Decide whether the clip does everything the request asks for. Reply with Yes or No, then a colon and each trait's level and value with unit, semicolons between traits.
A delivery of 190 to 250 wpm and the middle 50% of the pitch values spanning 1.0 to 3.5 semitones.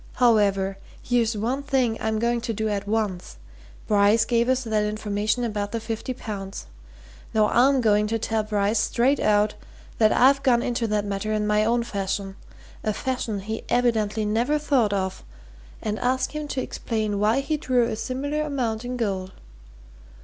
No: average, 170 wpm; average, 2.8 semitones